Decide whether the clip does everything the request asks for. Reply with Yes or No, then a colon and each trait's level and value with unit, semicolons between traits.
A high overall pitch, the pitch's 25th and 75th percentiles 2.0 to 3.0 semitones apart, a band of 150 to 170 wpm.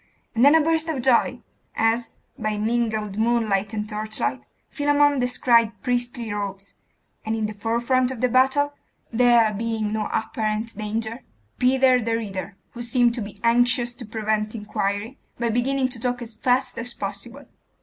Yes: high, 230 Hz; narrow, 2.5 semitones; average, 160 wpm